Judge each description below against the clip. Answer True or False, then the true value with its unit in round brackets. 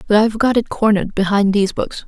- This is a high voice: True (210 Hz)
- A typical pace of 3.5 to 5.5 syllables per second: False (6.8 syllables/s)